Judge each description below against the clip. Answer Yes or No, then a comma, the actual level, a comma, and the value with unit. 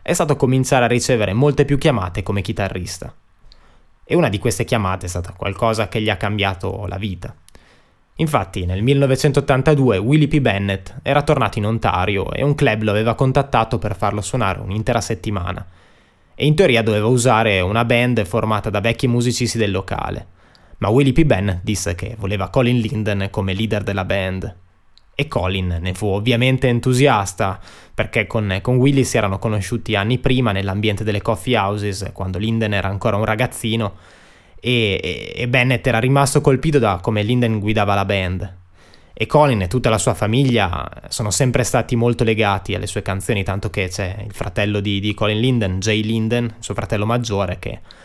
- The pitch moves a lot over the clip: No, average, 3.8 semitones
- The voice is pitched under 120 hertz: Yes, low, 110 Hz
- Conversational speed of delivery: No, fast, 175 wpm